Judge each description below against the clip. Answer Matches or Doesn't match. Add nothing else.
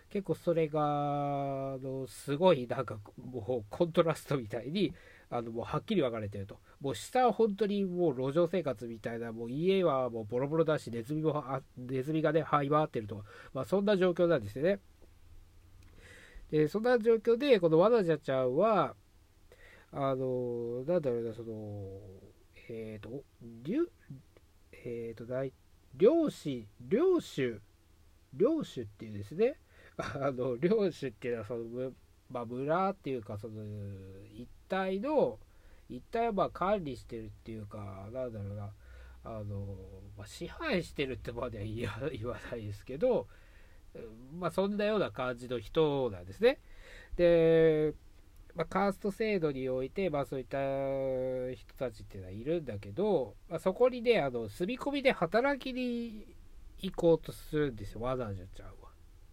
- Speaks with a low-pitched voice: Matches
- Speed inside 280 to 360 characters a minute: Matches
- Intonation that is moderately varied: Doesn't match